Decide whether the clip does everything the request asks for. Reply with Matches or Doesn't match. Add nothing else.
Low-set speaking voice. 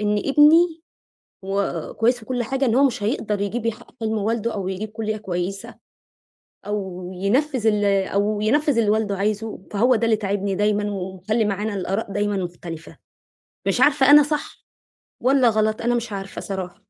Doesn't match